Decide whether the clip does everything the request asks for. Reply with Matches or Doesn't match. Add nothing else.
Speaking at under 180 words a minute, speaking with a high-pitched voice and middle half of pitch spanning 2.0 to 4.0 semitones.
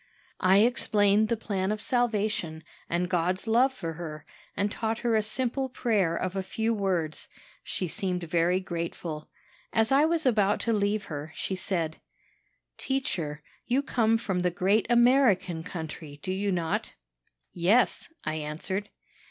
Doesn't match